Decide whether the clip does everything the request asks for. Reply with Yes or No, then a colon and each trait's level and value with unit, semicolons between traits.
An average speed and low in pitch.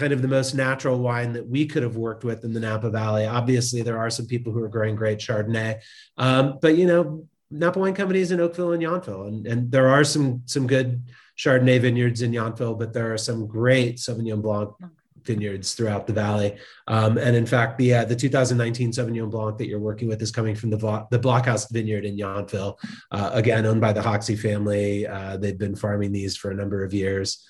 No: fast, 220 wpm; low, 115 Hz